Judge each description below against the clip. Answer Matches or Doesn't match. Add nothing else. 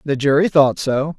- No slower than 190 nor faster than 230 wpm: Matches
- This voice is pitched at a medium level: Matches